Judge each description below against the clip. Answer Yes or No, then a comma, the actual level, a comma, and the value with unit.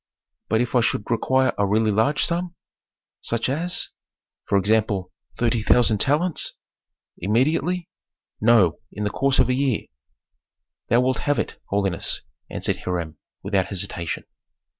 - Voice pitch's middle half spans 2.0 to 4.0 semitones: No, average, 5.2 semitones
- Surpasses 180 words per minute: No, average, 140 wpm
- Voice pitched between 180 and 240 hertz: No, low, 115 Hz